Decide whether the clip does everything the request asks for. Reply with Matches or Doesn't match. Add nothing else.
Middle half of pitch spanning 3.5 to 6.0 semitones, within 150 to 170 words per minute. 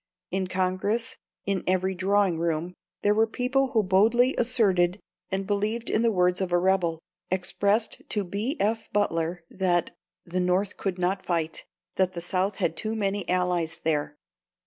Doesn't match